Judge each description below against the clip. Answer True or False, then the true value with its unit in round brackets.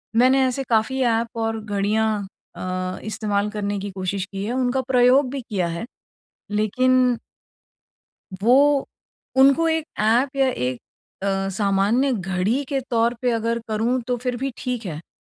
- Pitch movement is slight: False (4.1 semitones)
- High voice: True (230 Hz)